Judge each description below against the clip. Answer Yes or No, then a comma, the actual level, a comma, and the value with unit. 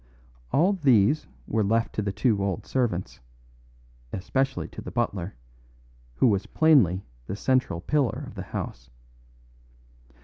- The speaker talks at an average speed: No, slow, 130 wpm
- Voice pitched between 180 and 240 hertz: No, low, 110 Hz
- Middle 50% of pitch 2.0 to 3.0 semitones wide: No, wide, 5.4 semitones